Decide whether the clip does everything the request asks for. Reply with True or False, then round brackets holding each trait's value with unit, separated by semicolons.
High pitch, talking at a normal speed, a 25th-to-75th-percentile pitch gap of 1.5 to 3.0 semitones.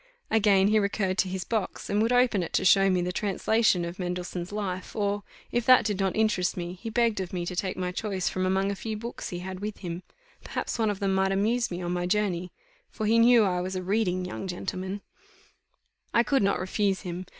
False (195 Hz; 230 wpm; 2.7 semitones)